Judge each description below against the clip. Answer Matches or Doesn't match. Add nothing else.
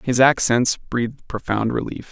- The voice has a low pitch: Matches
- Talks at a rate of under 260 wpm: Matches